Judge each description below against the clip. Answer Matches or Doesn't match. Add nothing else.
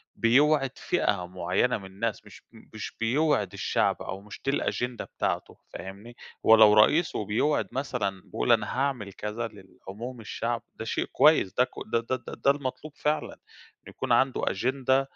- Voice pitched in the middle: Doesn't match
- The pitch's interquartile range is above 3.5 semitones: Matches